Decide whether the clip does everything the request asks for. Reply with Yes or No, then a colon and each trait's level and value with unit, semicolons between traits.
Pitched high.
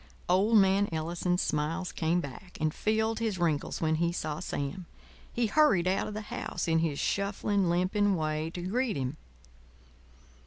No: medium, 180 Hz